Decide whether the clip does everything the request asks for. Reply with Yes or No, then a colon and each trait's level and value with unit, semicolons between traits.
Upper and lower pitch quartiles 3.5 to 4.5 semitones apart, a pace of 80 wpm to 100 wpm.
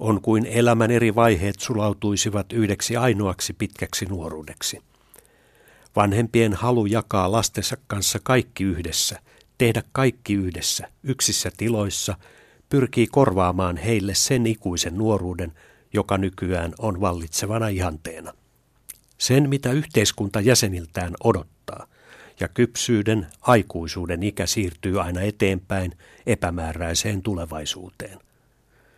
Yes: average, 3.9 semitones; slow, 95 wpm